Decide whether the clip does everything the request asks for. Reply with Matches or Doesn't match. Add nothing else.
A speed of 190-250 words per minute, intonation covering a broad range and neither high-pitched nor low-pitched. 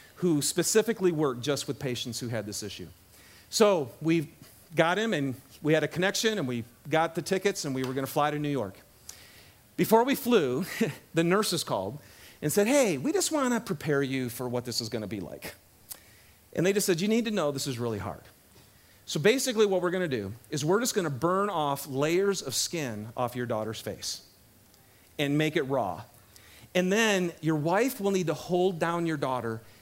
Matches